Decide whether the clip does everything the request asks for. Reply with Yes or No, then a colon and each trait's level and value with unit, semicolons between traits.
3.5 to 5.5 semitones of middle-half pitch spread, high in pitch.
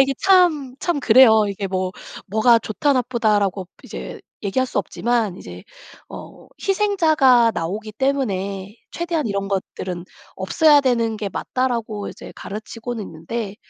Yes: average, 5.1 semitones; high, 230 Hz